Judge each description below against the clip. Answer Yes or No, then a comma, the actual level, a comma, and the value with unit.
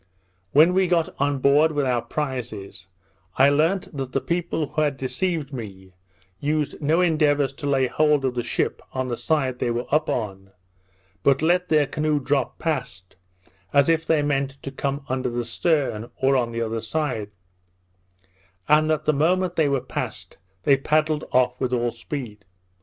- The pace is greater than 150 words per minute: Yes, average, 175 wpm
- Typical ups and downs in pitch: Yes, average, 3.7 semitones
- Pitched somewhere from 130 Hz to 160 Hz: Yes, medium, 140 Hz